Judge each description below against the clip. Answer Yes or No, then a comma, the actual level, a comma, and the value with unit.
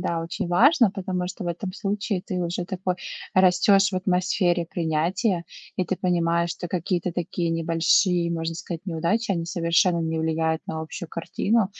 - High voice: No, medium, 175 Hz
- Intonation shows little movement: Yes, narrow, 2.0 semitones